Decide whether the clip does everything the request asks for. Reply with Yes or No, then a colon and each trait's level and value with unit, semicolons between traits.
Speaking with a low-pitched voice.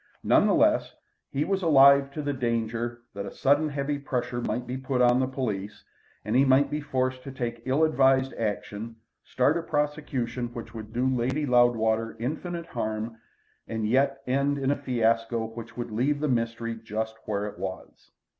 Yes: low, 125 Hz